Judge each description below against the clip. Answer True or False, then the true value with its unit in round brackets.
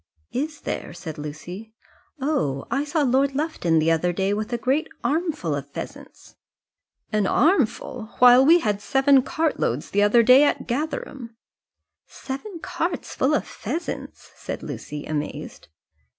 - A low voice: False (255 Hz)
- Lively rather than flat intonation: True (6.9 semitones)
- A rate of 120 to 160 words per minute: True (140 wpm)